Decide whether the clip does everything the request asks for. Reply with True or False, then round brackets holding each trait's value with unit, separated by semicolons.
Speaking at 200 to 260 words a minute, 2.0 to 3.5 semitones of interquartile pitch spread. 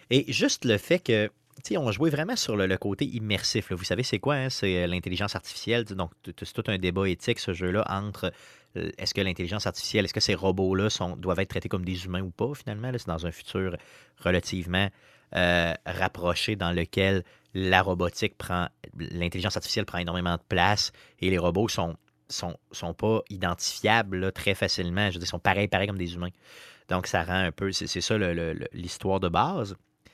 True (205 wpm; 2.8 semitones)